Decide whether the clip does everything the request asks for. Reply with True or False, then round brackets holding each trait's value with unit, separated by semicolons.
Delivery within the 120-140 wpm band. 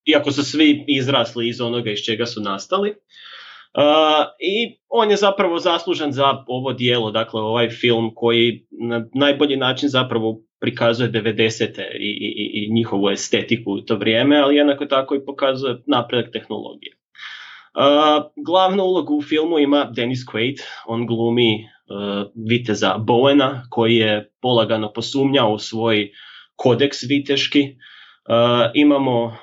True (135 wpm)